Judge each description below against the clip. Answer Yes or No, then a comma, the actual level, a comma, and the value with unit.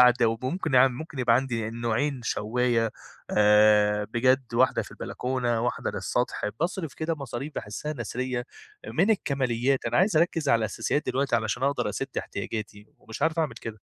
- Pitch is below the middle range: Yes, low, 125 Hz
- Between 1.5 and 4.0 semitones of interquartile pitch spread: Yes, average, 3.6 semitones